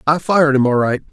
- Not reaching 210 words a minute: No, fast, 270 wpm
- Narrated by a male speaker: Yes, male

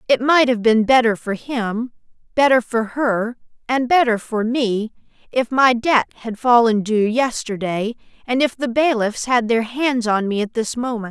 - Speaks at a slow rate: No, average, 180 wpm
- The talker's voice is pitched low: No, high, 235 Hz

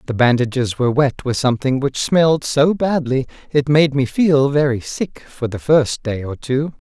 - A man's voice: Yes, male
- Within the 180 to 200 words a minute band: Yes, average, 190 wpm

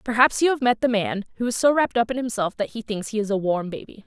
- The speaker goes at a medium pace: No, fast, 310 wpm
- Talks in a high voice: Yes, high, 225 Hz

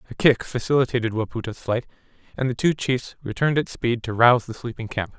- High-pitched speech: No, low, 120 Hz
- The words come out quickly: No, average, 195 wpm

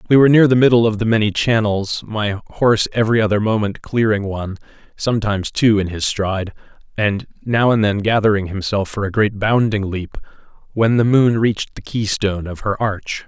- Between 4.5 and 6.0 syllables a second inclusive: Yes, 5.5 syllables/s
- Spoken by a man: Yes, male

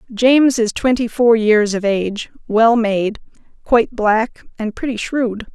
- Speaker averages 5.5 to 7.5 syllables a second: No, 4.2 syllables/s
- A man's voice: No, female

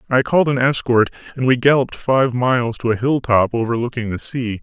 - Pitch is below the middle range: Yes, low, 125 Hz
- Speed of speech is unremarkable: Yes, average, 195 wpm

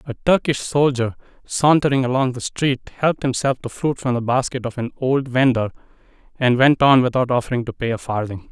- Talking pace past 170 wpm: Yes, average, 190 wpm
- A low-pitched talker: Yes, low, 130 Hz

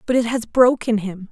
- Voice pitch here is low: No, high, 225 Hz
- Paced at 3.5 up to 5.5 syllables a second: Yes, 5.1 syllables/s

